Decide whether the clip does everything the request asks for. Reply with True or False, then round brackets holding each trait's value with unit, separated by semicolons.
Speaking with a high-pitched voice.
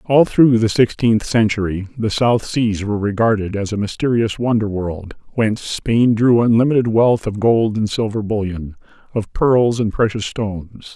False (110 Hz)